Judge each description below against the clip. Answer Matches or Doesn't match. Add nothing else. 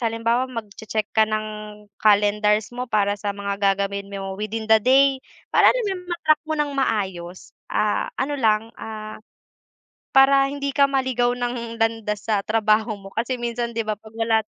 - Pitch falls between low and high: Doesn't match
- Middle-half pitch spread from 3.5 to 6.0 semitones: Doesn't match